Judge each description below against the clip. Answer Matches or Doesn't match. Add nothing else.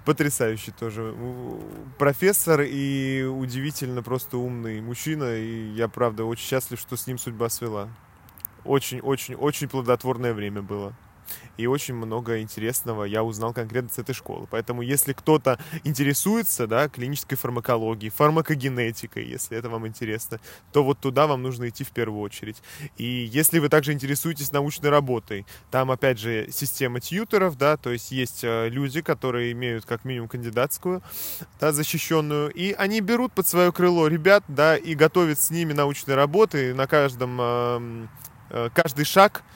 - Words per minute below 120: Doesn't match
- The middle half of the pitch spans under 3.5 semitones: Doesn't match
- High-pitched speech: Doesn't match